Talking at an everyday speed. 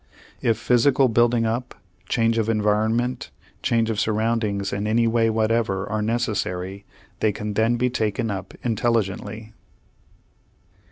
No: slow, 125 wpm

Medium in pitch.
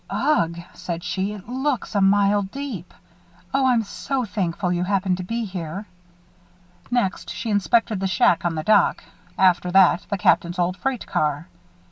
No: high, 195 Hz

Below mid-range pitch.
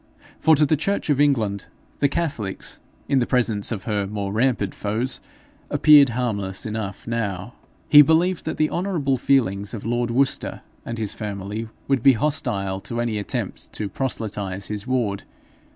Yes: low, 115 Hz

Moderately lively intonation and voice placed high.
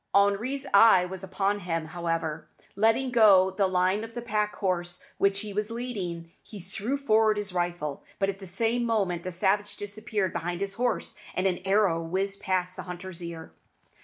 Yes: average, 3.2 semitones; high, 195 Hz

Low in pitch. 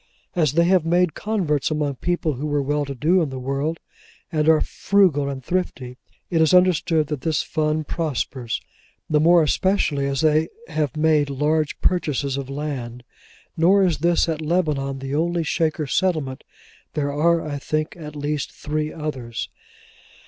No: medium, 155 Hz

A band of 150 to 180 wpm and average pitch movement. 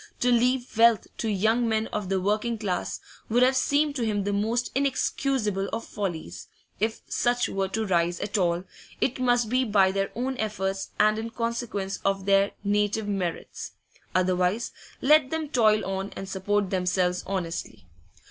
Yes: average, 165 wpm; average, 3.6 semitones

